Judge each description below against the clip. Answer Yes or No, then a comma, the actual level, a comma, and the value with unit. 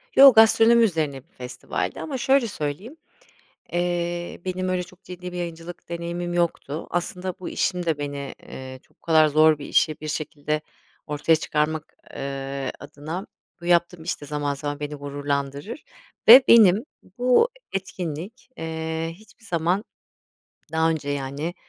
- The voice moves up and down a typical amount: Yes, average, 3.8 semitones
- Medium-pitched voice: Yes, medium, 165 Hz